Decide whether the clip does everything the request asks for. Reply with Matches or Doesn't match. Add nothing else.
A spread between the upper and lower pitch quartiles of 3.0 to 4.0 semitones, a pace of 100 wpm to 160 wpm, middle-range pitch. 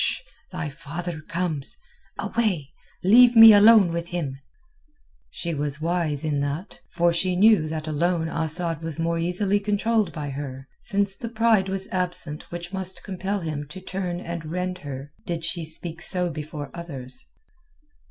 Matches